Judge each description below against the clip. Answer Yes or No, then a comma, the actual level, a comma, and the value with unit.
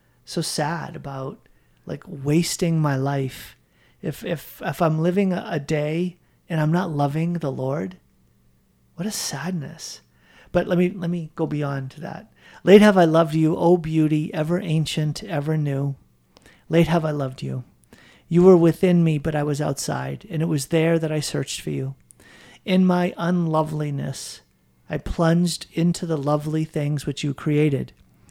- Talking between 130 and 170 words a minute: Yes, average, 165 wpm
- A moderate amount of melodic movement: Yes, average, 3.3 semitones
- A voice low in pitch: No, medium, 155 Hz